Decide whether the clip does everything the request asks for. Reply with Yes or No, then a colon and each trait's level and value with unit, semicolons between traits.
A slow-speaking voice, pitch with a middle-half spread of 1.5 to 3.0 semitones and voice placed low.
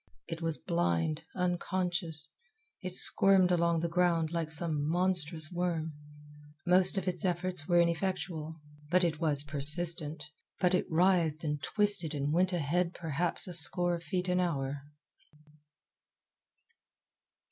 No: slow, 130 wpm; narrow, 2.5 semitones; medium, 170 Hz